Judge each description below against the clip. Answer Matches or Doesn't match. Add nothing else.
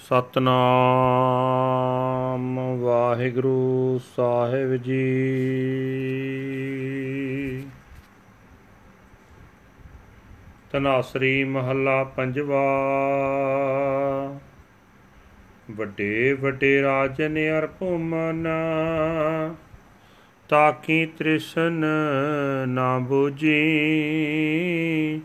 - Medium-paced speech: Doesn't match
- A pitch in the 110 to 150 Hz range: Matches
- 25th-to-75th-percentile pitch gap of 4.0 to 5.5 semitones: Doesn't match